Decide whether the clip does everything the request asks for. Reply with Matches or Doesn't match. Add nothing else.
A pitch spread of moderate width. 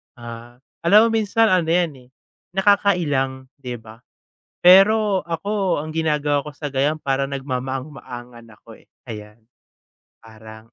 Doesn't match